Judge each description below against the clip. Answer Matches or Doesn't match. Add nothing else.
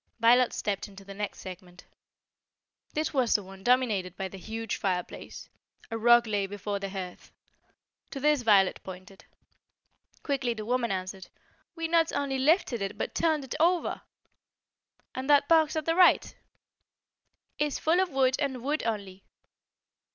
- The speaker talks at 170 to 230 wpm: Doesn't match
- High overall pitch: Matches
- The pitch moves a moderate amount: Doesn't match